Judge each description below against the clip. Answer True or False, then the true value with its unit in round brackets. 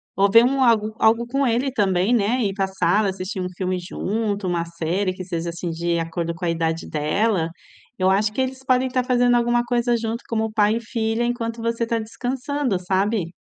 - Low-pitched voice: False (215 Hz)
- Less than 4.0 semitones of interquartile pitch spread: False (4.6 semitones)